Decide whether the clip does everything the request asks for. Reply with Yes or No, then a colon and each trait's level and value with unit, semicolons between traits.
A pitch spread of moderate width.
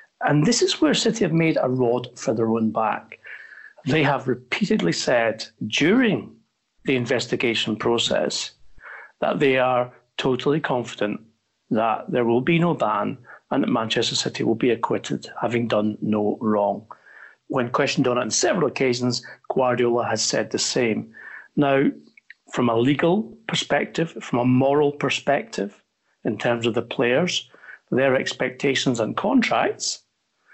Yes: average, 3.5 semitones